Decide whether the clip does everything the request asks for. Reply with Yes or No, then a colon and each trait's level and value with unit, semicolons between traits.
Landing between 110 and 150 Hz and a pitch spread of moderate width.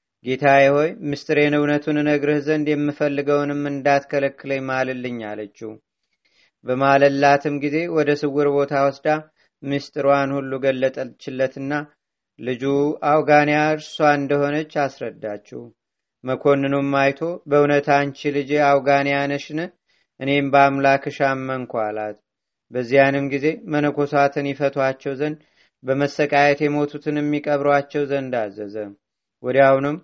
No: medium, 140 Hz; narrow, 1.4 semitones